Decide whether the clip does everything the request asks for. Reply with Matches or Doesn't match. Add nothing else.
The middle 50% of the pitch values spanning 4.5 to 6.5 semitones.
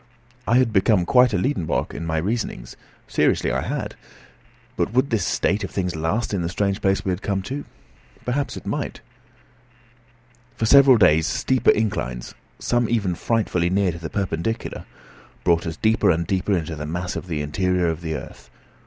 Matches